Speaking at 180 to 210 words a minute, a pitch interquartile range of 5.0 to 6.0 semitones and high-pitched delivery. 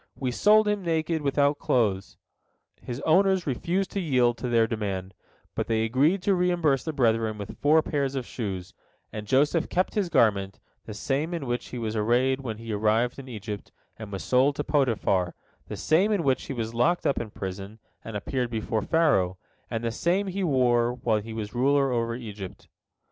No: average, 190 wpm; wide, 5.6 semitones; low, 125 Hz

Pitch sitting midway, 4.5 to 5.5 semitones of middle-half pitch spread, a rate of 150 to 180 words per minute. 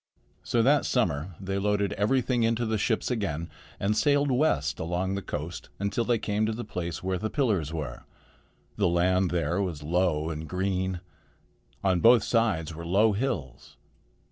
No: very low, 95 Hz; average, 4.8 semitones; average, 165 wpm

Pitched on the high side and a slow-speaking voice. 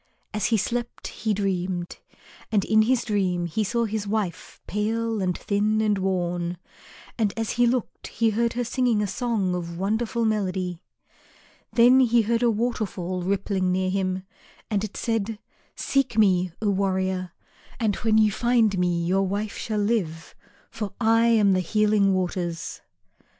No: high, 205 Hz; average, 155 wpm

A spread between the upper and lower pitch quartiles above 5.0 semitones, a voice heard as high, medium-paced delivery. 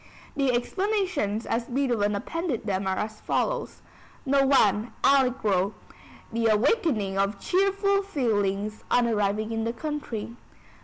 No: wide, 5.5 semitones; high, 230 Hz; slow, 120 wpm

